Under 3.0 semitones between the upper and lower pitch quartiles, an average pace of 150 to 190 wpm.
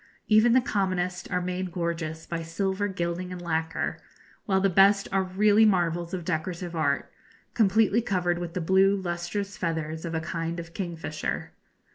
Yes: narrow, 2.5 semitones; average, 160 wpm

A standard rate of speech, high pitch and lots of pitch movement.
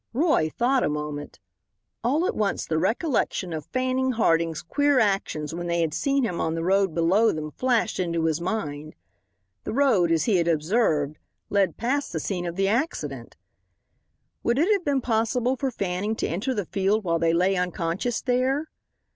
Yes: average, 180 wpm; high, 195 Hz; wide, 7.1 semitones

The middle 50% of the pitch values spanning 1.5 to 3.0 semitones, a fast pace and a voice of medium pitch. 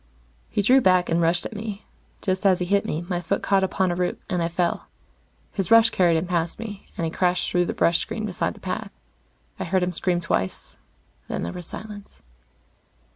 Yes: narrow, 2.5 semitones; fast, 210 wpm; medium, 180 Hz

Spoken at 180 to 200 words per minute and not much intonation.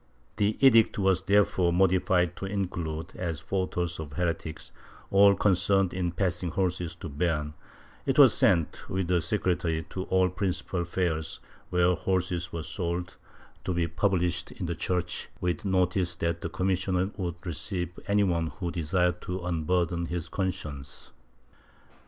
No: average, 145 wpm; narrow, 1.9 semitones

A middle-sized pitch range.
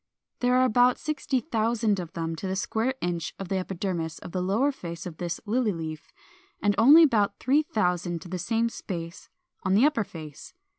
No: wide, 5.8 semitones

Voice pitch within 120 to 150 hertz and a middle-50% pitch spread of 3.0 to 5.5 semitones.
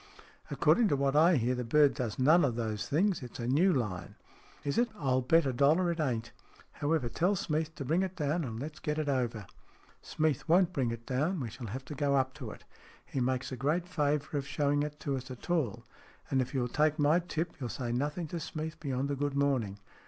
Yes: medium, 140 Hz; average, 3.9 semitones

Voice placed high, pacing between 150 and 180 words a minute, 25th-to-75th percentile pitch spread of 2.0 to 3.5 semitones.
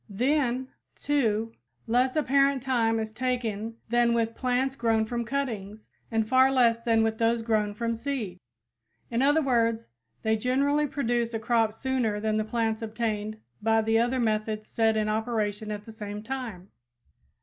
Yes: high, 230 Hz; average, 160 wpm; narrow, 2.5 semitones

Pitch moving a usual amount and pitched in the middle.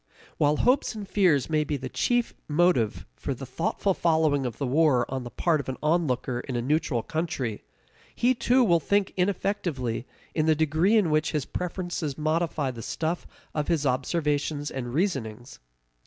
Yes: average, 4.8 semitones; medium, 155 Hz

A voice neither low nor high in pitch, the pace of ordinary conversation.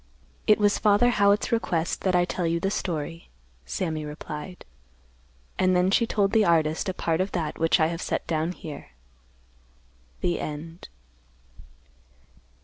Yes: medium, 175 Hz; average, 145 wpm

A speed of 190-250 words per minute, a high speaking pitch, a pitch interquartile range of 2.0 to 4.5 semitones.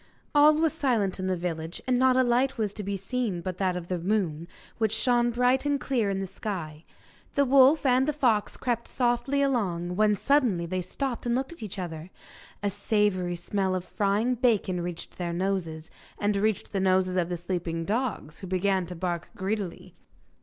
No: average, 195 wpm; high, 200 Hz; wide, 5.6 semitones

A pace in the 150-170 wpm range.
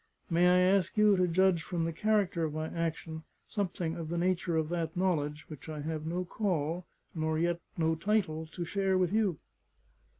No: average, 190 wpm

